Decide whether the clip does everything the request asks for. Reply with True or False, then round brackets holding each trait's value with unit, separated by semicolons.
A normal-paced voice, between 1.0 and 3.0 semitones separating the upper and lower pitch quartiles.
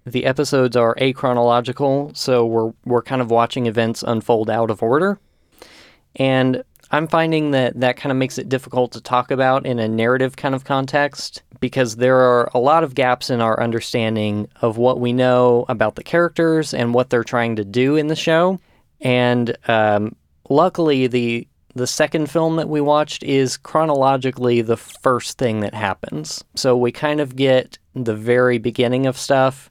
True (175 wpm; 2.4 semitones)